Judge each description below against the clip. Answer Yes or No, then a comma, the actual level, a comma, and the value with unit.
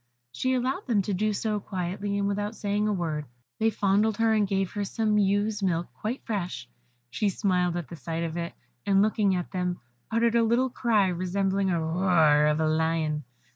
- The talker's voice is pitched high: Yes, high, 195 Hz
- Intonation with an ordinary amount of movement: Yes, average, 3.6 semitones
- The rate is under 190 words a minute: No, average, 195 wpm